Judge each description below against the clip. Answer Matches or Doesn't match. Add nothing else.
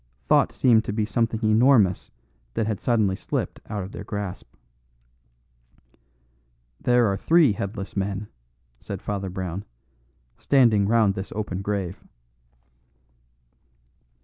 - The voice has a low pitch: Matches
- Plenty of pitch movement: Doesn't match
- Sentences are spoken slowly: Matches